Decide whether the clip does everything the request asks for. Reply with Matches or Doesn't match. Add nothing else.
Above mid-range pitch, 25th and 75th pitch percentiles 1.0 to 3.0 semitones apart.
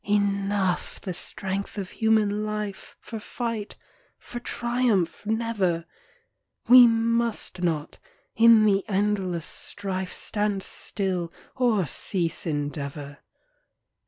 Doesn't match